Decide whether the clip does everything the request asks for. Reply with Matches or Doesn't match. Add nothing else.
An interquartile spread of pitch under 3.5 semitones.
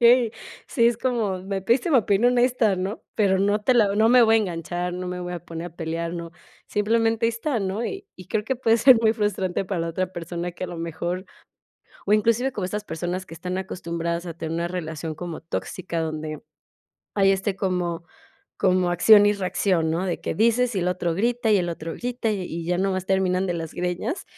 Doesn't match